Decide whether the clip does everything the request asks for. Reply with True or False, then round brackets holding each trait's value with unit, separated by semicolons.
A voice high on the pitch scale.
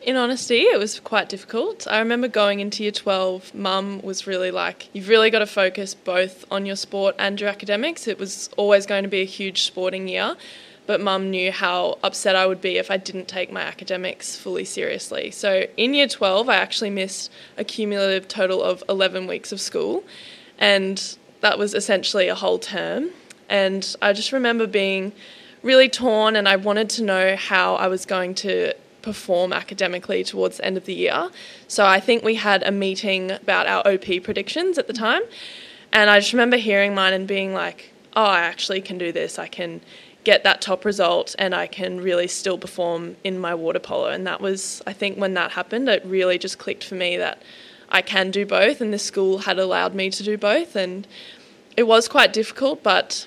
True (195 Hz)